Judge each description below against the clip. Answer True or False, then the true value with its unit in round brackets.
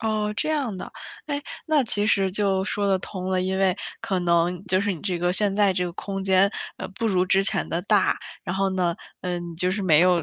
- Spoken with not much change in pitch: True (2.2 semitones)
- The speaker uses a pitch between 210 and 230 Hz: False (190 Hz)